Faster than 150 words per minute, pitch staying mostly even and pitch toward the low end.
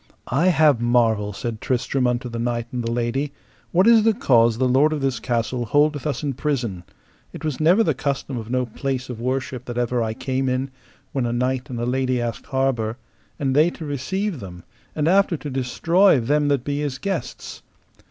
No: average, 200 wpm; average, 3.6 semitones; low, 130 Hz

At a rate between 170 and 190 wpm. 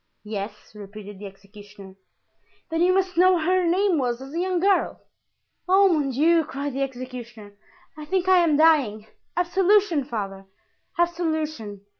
No: average, 150 wpm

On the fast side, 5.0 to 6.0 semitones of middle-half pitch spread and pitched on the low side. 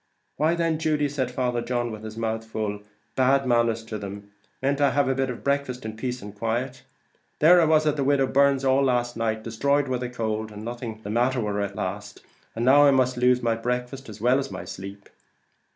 No: fast, 220 wpm; average, 3.6 semitones; low, 125 Hz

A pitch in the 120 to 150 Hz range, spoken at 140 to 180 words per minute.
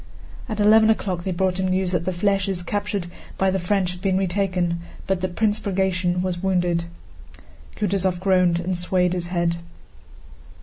No: medium, 185 Hz; average, 165 wpm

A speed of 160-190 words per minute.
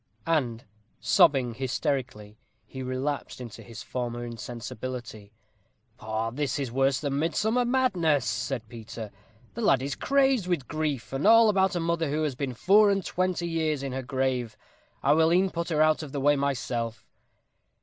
Yes: average, 165 wpm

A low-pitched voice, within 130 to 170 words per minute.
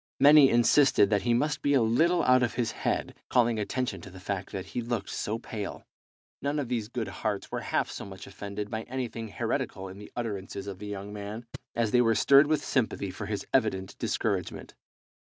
No: low, 115 Hz; fast, 205 wpm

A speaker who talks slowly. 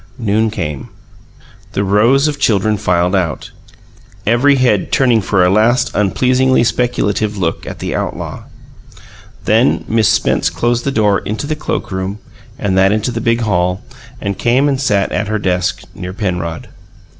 No: average, 155 wpm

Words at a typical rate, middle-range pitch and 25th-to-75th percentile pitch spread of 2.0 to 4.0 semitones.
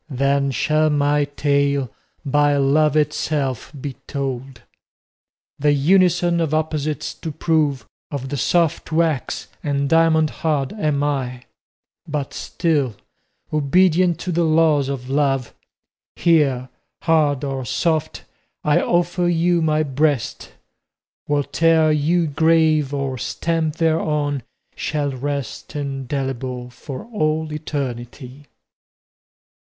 No: slow, 105 wpm; medium, 145 Hz; narrow, 2.5 semitones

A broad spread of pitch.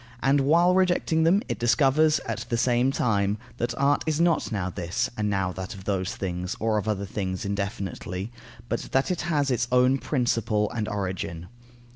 Yes: wide, 5.9 semitones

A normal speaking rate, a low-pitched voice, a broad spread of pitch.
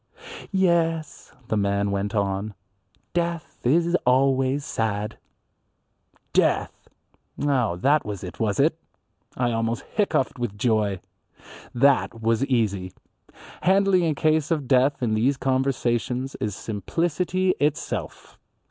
No: slow, 110 wpm; low, 125 Hz; wide, 5.7 semitones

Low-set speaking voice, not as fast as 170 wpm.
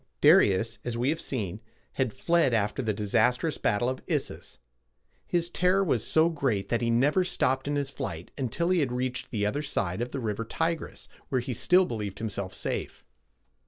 No: low, 125 Hz; average, 185 wpm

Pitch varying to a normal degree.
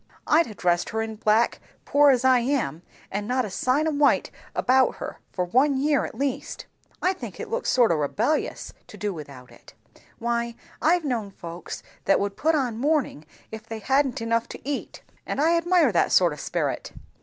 No: wide, 5.8 semitones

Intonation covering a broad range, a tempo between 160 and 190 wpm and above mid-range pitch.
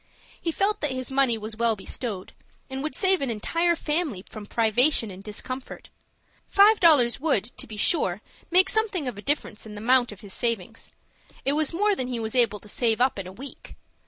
No: wide, 6.2 semitones; fast, 205 wpm; very high, 250 Hz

